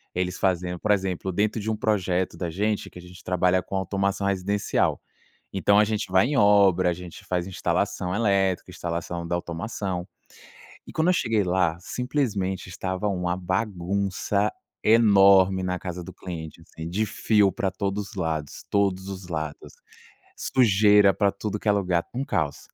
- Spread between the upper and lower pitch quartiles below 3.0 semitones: Yes, narrow, 2.4 semitones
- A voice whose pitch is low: Yes, very low, 95 Hz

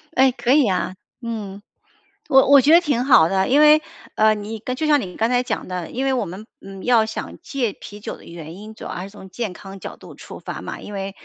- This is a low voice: No, high, 220 Hz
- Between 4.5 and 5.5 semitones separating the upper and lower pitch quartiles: Yes, average, 5.1 semitones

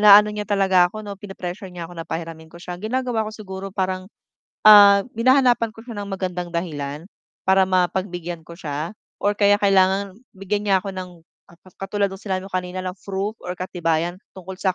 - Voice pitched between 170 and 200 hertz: Yes, high, 190 Hz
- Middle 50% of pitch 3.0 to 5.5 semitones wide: No, narrow, 2.4 semitones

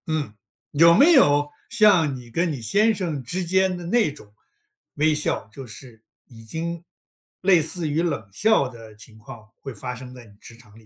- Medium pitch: Yes, medium, 145 Hz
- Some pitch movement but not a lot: No, wide, 6.7 semitones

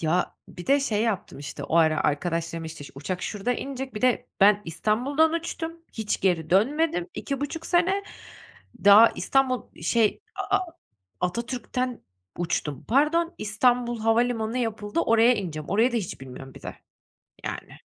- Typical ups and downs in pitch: No, wide, 6.9 semitones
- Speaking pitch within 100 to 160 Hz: No, high, 225 Hz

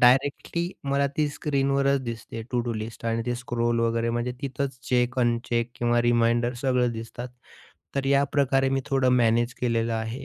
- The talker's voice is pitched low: Yes, low, 120 Hz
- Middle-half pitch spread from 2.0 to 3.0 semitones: Yes, narrow, 2.5 semitones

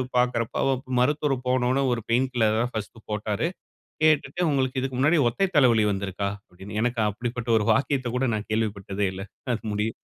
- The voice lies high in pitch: No, low, 120 Hz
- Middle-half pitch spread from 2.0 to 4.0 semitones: Yes, average, 3.7 semitones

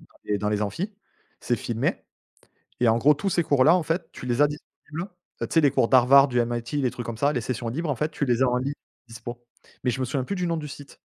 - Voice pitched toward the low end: Yes, low, 130 Hz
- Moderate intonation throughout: Yes, average, 4.0 semitones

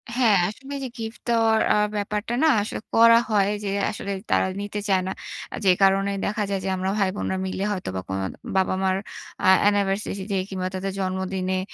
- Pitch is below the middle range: No, high, 195 Hz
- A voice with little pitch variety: Yes, narrow, 2.0 semitones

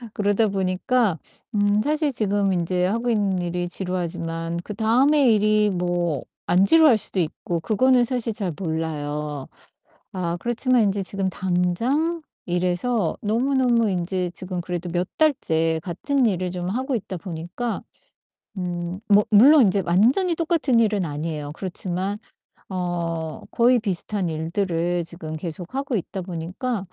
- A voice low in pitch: No, high, 190 Hz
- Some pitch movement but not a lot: Yes, average, 4.8 semitones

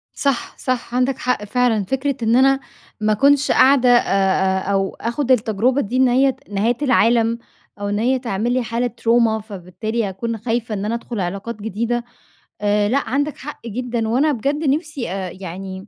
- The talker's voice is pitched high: Yes, high, 235 Hz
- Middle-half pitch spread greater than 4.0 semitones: No, average, 3.5 semitones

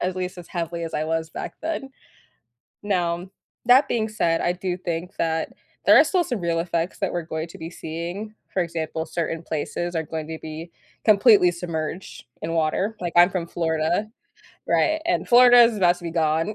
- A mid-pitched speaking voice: Yes, medium, 175 Hz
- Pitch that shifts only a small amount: No, average, 3.2 semitones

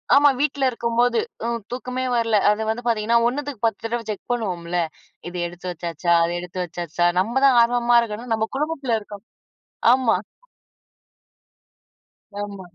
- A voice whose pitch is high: Yes, high, 230 Hz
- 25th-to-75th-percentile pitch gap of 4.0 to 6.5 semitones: Yes, average, 4.5 semitones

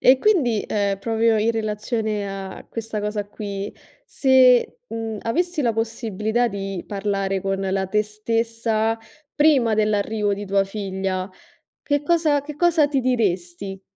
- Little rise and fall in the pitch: No, average, 3.3 semitones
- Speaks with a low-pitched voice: No, high, 215 Hz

